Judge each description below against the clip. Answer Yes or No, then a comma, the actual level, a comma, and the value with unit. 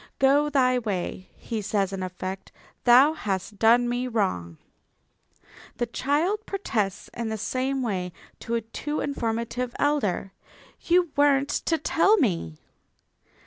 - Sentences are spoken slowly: Yes, slow, 130 wpm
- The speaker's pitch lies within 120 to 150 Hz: No, high, 240 Hz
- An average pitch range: No, wide, 6.2 semitones